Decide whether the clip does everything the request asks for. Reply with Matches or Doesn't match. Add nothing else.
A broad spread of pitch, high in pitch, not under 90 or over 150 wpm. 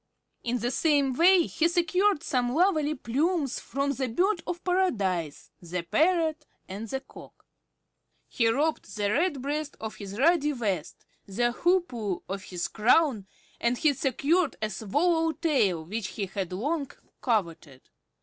Matches